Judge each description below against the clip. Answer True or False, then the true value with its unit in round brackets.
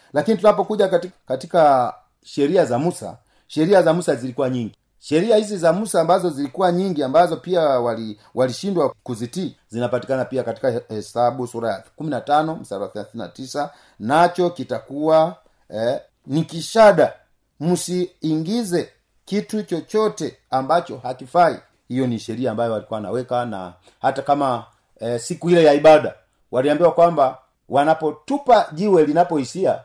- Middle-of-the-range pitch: True (150 Hz)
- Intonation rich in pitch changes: True (5.8 semitones)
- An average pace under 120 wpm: False (125 wpm)